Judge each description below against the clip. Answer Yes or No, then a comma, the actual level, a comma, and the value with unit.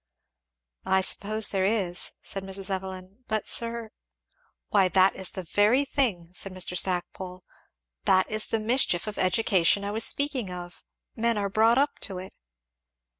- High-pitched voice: Yes, high, 195 Hz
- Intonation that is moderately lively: Yes, average, 3.1 semitones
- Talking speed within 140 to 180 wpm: Yes, average, 160 wpm